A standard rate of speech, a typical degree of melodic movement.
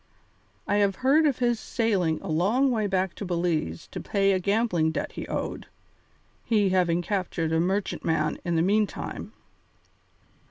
Yes: average, 155 wpm; average, 4.2 semitones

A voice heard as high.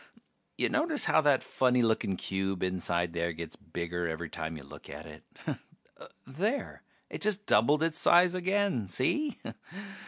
No: low, 115 Hz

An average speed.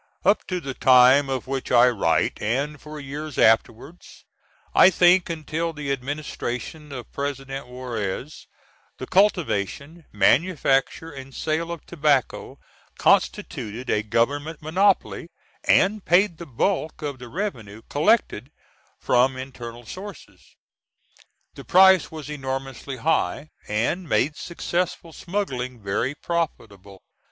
No: slow, 115 wpm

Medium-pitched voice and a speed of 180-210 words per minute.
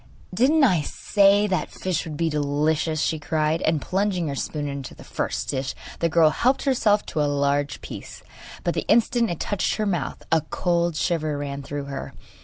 Yes: medium, 160 Hz; average, 185 wpm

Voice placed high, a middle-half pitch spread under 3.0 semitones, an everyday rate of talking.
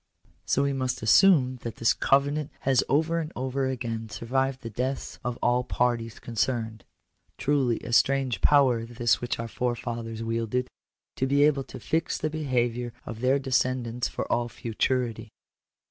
No: low, 125 Hz; narrow, 2.6 semitones; average, 160 wpm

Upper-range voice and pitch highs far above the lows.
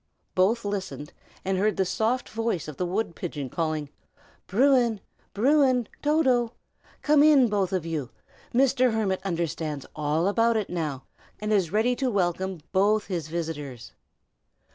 Yes: high, 195 Hz; wide, 5.9 semitones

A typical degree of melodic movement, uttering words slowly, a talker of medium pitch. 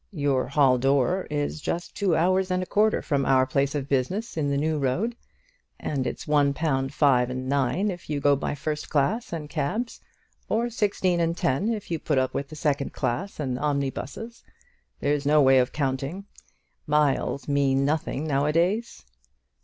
No: average, 4.2 semitones; average, 180 wpm; medium, 145 Hz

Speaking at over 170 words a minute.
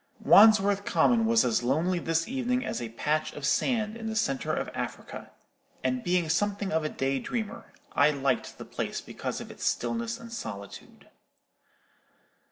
No: average, 165 wpm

